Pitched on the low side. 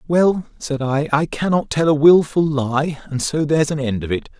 No: medium, 150 Hz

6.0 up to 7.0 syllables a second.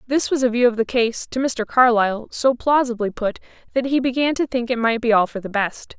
No: 5.6 syllables/s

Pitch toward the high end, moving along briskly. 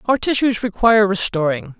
No: high, 210 Hz; slow, 135 wpm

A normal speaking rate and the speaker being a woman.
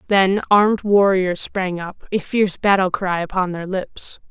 Yes: average, 165 wpm; female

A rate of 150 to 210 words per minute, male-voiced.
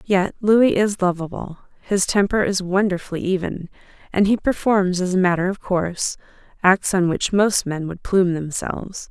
No: average, 165 wpm; female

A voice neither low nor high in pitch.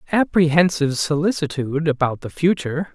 Yes: medium, 155 Hz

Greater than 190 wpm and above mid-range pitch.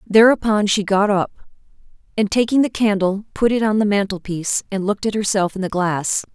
Yes: average, 200 wpm; high, 205 Hz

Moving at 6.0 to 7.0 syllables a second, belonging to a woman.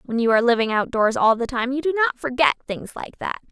Yes: 6.2 syllables/s; female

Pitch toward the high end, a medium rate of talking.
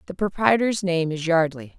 No: medium, 175 Hz; average, 170 wpm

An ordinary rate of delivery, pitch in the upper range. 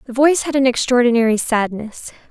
Yes: average, 155 wpm; high, 245 Hz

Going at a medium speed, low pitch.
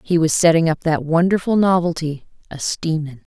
No: average, 160 wpm; medium, 165 Hz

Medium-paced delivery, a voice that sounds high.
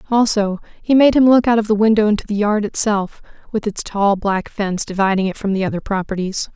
No: fast, 220 wpm; high, 210 Hz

